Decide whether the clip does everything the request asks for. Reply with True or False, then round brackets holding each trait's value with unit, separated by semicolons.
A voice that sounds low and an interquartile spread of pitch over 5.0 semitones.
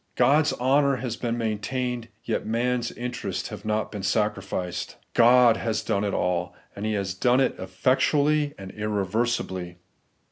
False (115 Hz; 3.9 semitones)